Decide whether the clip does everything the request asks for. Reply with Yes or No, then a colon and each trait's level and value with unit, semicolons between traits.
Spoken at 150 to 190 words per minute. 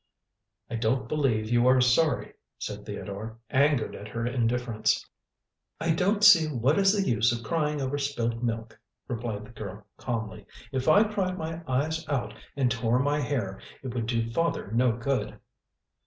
Yes: average, 165 wpm